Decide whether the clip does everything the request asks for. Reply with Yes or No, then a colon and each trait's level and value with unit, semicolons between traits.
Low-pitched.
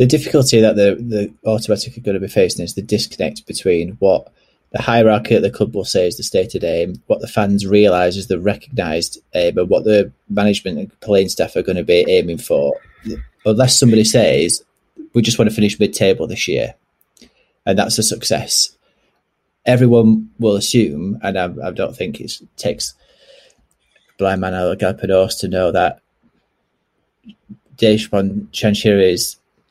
Yes: low, 110 Hz